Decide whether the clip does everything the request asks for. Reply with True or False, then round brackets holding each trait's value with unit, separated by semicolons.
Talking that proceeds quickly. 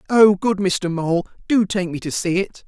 True (225 wpm)